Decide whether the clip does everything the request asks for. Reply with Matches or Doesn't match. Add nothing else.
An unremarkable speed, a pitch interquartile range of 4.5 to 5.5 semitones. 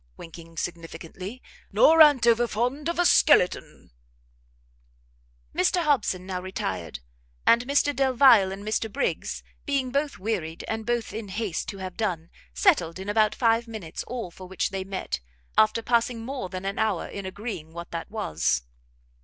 Matches